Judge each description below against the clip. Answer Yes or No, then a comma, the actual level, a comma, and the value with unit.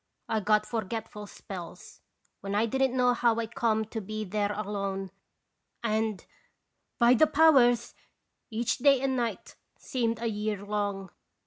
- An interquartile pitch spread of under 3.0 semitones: Yes, narrow, 2.6 semitones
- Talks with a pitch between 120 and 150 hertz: No, high, 220 Hz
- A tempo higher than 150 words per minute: No, average, 140 wpm